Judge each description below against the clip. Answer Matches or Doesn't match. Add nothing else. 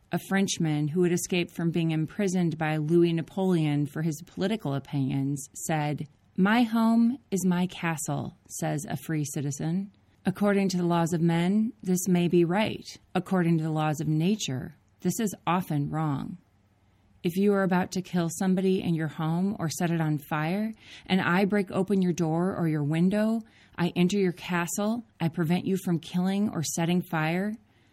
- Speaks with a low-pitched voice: Doesn't match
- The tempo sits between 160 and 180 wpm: Matches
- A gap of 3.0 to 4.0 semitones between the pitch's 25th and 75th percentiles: Matches